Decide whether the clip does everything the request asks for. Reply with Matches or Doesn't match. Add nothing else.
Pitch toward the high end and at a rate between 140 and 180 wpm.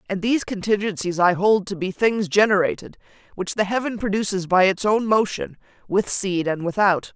Matches